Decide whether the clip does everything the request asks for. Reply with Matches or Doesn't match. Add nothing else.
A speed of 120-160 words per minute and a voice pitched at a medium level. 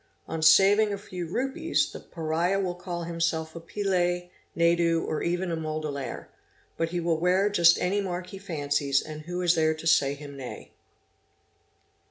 Doesn't match